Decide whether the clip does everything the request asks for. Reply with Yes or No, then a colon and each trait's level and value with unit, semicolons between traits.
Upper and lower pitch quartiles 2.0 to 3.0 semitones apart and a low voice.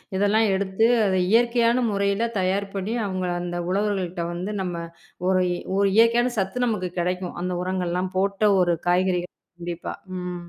No: average, 2.7 semitones; high, 190 Hz